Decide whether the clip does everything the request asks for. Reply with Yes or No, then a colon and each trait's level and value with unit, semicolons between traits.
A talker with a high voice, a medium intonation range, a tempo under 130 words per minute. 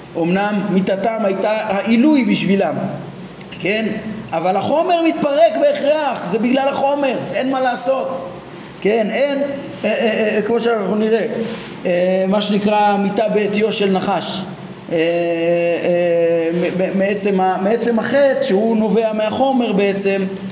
Yes: high, 210 Hz; average, 3.9 semitones; average, 115 wpm